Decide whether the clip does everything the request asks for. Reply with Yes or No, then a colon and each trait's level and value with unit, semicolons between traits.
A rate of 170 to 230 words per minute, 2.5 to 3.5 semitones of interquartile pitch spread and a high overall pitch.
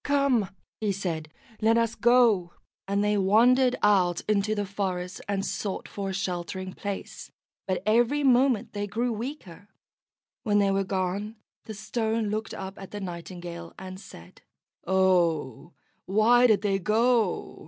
No: average, 145 wpm; average, 3.1 semitones; high, 200 Hz